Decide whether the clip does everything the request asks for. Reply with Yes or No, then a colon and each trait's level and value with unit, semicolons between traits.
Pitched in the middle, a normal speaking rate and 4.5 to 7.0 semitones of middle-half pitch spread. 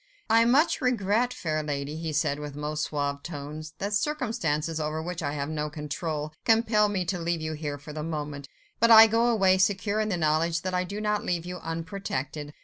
No: medium, 165 Hz; fast, 210 wpm; average, 5.3 semitones